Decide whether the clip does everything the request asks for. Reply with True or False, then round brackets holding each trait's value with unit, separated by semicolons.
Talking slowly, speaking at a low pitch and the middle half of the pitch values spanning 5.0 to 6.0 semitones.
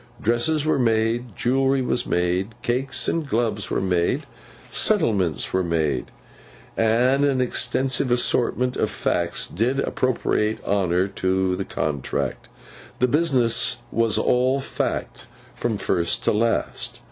True (125 wpm; 115 Hz; 5.4 semitones)